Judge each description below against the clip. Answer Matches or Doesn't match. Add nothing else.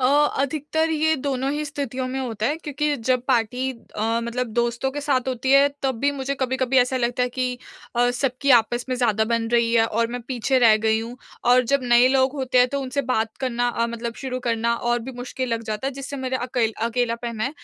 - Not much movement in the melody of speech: Matches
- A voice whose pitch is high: Matches